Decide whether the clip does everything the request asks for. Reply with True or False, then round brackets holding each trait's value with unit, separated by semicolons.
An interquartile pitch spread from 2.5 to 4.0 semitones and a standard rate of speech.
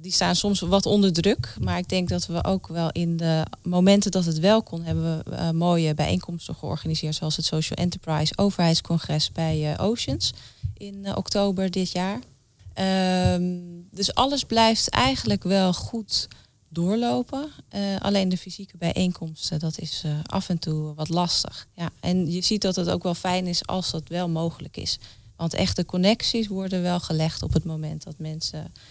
True (3.2 semitones; 180 wpm)